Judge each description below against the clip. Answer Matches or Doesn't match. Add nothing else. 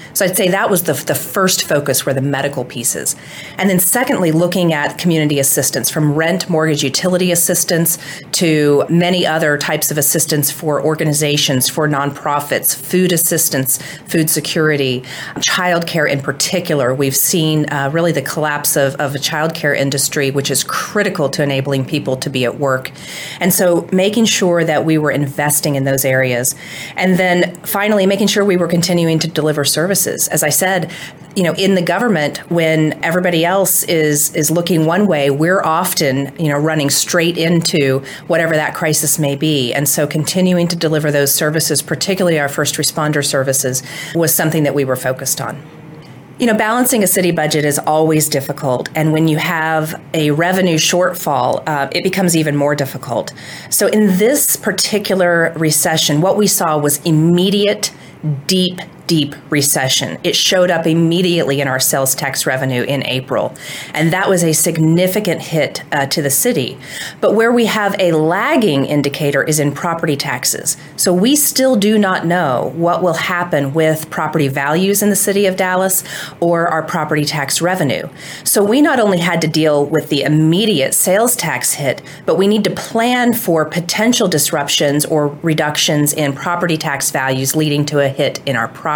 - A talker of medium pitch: Matches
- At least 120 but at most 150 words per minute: Doesn't match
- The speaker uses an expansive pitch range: Doesn't match